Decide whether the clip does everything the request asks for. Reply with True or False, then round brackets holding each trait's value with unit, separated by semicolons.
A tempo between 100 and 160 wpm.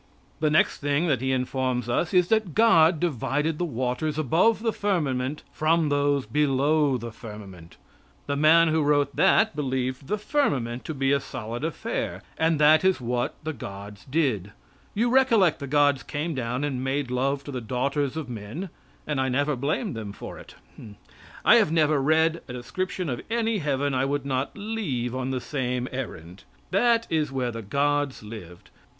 False (175 wpm)